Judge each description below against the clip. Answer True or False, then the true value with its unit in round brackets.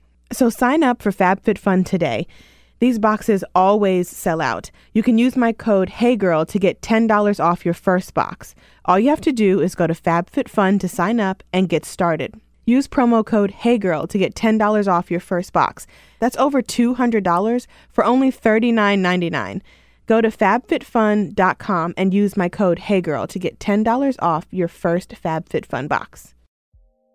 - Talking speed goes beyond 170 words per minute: False (160 wpm)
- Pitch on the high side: True (200 Hz)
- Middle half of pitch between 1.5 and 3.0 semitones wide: False (4.7 semitones)